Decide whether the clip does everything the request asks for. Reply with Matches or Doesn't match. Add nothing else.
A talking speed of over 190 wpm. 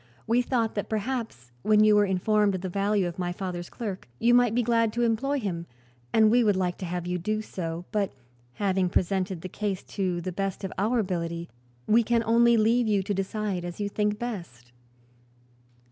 Matches